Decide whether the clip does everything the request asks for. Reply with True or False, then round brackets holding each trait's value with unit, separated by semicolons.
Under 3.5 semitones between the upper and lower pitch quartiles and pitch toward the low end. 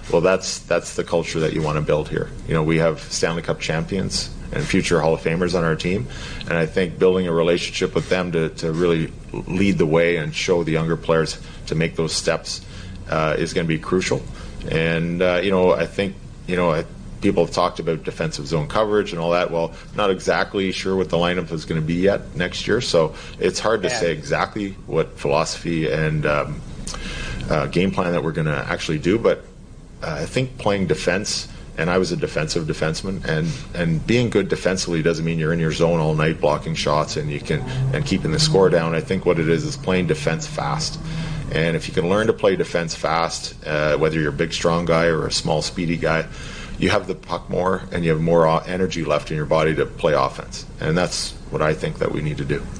True (3.0 semitones; 85 Hz)